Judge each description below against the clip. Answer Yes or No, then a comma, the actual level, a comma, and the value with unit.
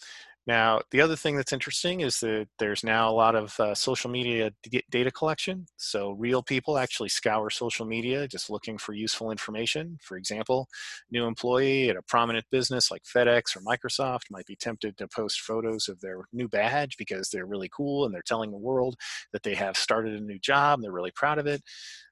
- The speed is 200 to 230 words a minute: Yes, fast, 205 wpm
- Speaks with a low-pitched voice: Yes, low, 120 Hz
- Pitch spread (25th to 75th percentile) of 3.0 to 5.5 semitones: Yes, average, 3.5 semitones